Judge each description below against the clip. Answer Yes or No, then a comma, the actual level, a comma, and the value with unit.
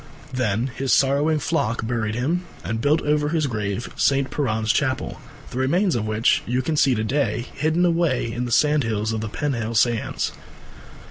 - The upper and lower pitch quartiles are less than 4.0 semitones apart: No, average, 4.9 semitones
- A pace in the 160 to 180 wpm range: Yes, average, 175 wpm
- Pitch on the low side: Yes, low, 130 Hz